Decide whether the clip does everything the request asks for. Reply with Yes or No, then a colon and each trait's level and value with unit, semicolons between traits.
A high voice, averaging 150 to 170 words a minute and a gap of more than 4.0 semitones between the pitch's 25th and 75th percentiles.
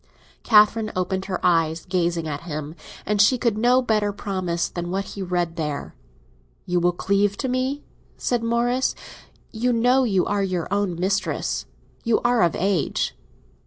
Yes: high, 195 Hz; average, 160 wpm; average, 4.7 semitones